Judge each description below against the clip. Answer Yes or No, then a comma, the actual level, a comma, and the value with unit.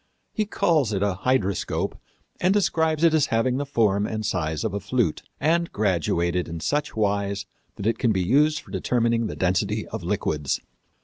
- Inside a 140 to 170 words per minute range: No, average, 180 wpm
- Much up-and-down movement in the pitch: Yes, wide, 6.6 semitones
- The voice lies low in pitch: Yes, low, 110 Hz